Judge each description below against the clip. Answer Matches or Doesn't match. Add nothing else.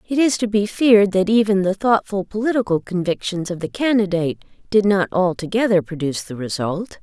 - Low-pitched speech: Doesn't match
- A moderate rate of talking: Matches